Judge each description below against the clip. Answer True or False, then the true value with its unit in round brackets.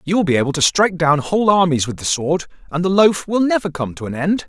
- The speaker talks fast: True (280 wpm)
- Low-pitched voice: False (170 Hz)